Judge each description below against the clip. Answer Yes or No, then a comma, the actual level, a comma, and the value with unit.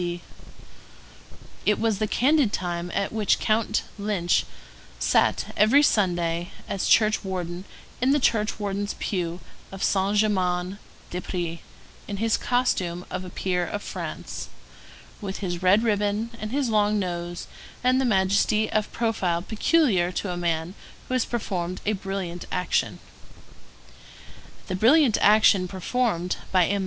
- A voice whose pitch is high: Yes, high, 200 Hz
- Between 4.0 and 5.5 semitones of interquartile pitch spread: No, average, 3.4 semitones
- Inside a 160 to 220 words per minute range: No, average, 140 wpm